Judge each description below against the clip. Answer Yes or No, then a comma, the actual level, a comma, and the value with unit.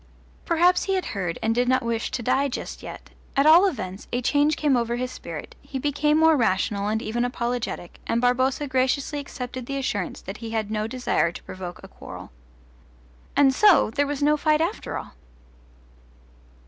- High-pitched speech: Yes, very high, 255 Hz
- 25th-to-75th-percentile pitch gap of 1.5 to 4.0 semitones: No, average, 4.5 semitones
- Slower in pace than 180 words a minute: No, average, 185 wpm